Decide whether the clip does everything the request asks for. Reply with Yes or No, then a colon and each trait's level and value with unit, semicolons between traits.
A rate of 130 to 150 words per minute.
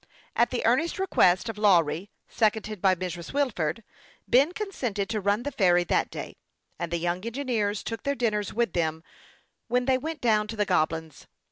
No: average, 175 wpm